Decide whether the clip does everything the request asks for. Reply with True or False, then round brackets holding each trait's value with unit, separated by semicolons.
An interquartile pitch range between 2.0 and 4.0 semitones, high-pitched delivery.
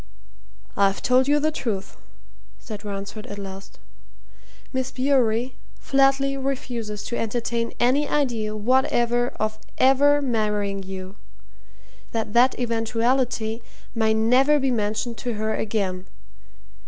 True (3.5 semitones; 230 Hz)